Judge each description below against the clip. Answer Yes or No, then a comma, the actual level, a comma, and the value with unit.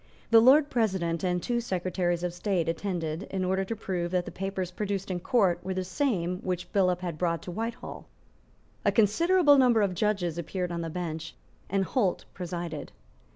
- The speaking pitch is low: No, medium, 185 Hz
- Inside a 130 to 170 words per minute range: No, average, 185 wpm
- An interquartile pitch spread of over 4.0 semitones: No, average, 3.0 semitones